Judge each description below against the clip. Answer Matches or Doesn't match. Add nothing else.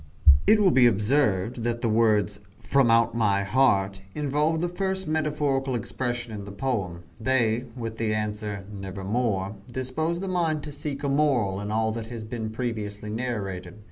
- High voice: Doesn't match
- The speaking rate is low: Doesn't match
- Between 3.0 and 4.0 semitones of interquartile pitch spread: Doesn't match